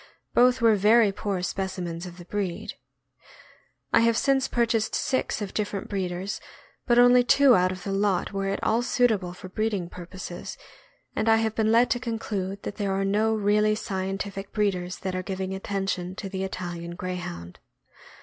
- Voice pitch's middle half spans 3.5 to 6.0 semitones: No, average, 3.1 semitones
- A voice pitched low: No, high, 195 Hz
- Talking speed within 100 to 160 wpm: No, average, 170 wpm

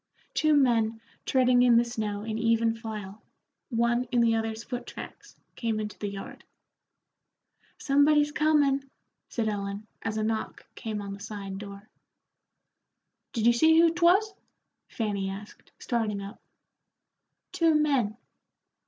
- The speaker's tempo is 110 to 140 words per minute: Yes, slow, 135 wpm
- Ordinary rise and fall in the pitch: Yes, average, 4.2 semitones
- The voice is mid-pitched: No, high, 230 Hz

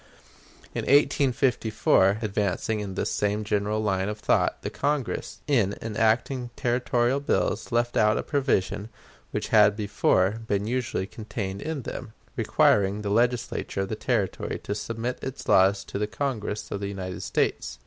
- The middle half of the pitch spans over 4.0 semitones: No, average, 3.2 semitones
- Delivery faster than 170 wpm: No, average, 150 wpm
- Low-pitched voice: Yes, low, 110 Hz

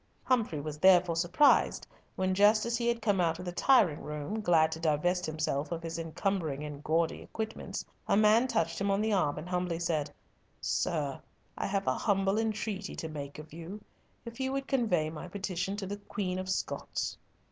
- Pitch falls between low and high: Yes, medium, 180 Hz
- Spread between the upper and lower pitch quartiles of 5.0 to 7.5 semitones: No, average, 4.5 semitones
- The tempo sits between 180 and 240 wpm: Yes, average, 190 wpm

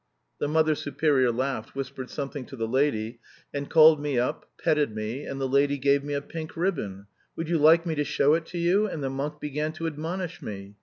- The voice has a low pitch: No, medium, 145 Hz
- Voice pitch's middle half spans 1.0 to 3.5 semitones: Yes, average, 3.1 semitones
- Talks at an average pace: No, fast, 215 wpm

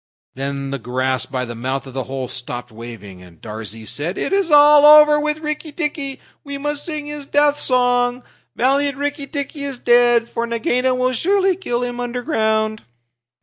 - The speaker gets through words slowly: No, average, 175 wpm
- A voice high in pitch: Yes, high, 245 Hz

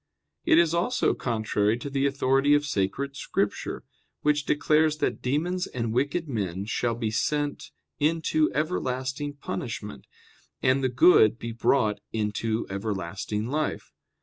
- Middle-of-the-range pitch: No, low, 130 Hz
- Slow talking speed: Yes, slow, 125 wpm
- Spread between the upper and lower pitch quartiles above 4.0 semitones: Yes, average, 5.2 semitones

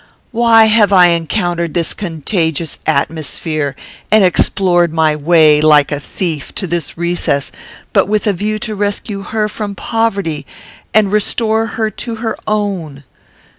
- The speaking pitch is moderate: Yes, medium, 180 Hz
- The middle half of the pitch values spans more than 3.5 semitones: Yes, average, 5.0 semitones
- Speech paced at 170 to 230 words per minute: No, average, 140 wpm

